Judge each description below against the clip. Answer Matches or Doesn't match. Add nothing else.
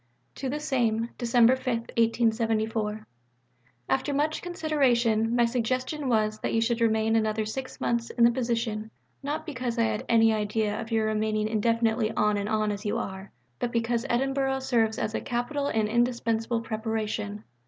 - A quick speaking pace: Doesn't match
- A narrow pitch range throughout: Matches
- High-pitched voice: Matches